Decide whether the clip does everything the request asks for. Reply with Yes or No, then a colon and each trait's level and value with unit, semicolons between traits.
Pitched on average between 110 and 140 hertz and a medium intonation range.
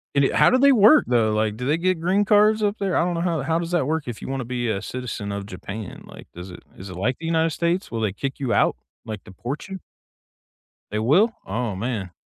No: low, 135 Hz; wide, 8.3 semitones